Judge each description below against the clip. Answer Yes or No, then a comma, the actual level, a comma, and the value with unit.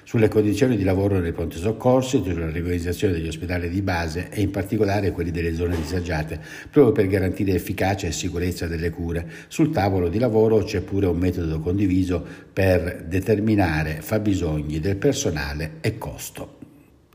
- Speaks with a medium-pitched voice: No, very low, 95 Hz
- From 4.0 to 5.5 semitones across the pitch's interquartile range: No, average, 3.5 semitones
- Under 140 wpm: No, average, 155 wpm